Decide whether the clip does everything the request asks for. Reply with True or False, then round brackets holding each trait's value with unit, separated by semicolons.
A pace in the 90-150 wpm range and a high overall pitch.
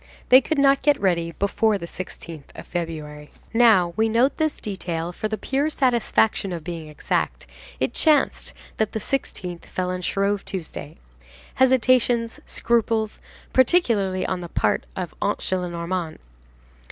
True (140 wpm; 200 Hz)